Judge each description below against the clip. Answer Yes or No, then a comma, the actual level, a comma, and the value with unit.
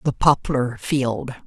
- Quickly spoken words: No, slow, 125 wpm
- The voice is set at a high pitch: No, low, 130 Hz